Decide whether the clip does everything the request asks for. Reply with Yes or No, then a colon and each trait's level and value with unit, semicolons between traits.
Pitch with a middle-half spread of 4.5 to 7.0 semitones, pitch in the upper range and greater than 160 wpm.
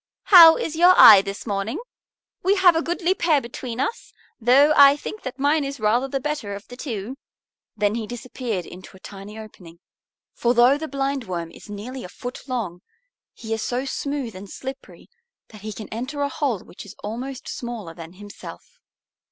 Yes: wide, 5.4 semitones; high, 245 Hz; average, 185 wpm